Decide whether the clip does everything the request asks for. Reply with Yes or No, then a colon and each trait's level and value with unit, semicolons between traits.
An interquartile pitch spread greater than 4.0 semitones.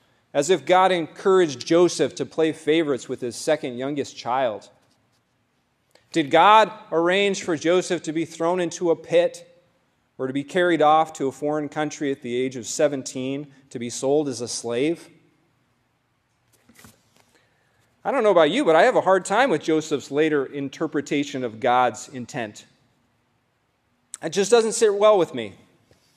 Yes: average, 4.9 semitones